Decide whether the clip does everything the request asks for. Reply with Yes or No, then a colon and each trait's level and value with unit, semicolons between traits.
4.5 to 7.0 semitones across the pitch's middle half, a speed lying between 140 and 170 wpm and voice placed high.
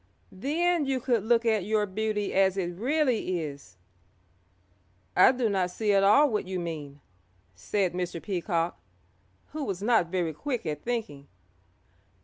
Yes: average, 5.2 semitones; average, 145 wpm; high, 200 Hz